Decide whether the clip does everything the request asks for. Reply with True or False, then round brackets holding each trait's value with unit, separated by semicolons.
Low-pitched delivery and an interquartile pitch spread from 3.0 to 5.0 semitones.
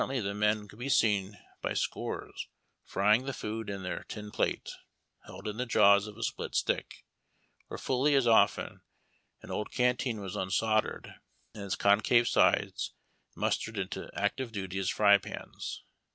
False (105 Hz; 2.6 semitones)